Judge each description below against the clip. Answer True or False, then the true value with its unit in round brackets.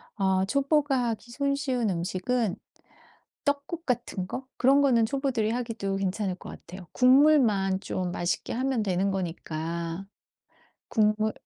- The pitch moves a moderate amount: False (5.8 semitones)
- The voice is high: True (220 Hz)